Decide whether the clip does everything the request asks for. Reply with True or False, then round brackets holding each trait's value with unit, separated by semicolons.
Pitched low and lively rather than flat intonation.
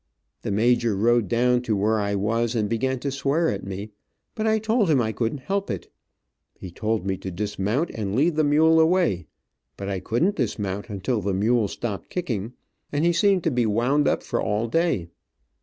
True (115 Hz; 6.4 semitones)